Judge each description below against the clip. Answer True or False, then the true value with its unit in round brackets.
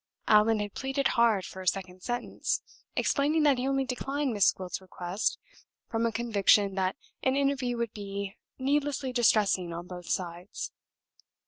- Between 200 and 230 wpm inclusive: False (150 wpm)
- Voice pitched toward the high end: True (220 Hz)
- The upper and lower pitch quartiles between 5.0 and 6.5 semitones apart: True (5.6 semitones)